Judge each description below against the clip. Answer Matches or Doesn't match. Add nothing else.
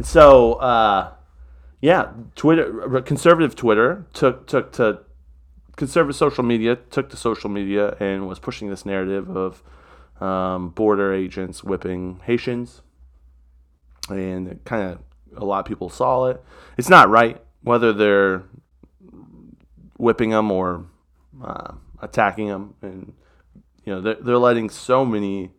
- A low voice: Matches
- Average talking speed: Doesn't match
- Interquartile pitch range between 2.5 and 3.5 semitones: Doesn't match